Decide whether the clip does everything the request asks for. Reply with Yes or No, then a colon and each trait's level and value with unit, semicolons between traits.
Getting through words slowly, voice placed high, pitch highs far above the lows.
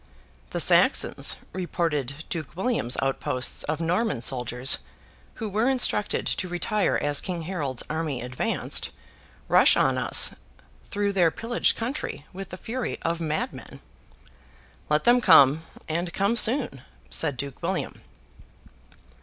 No: slow, 125 wpm; medium, 170 Hz; wide, 6.3 semitones